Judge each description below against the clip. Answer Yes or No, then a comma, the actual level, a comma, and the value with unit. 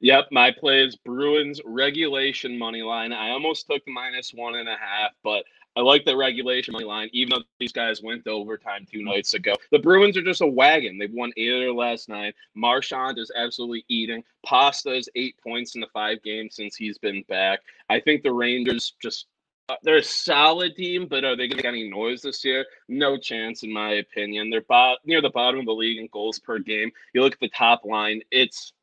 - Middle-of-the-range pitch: No, low, 120 Hz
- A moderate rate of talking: No, fast, 220 wpm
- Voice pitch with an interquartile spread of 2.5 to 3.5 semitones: Yes, average, 3.2 semitones